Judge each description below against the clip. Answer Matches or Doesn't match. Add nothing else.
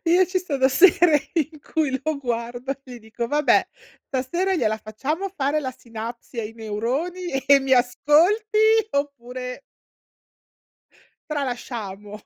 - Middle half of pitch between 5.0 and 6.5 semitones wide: Matches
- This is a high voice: Matches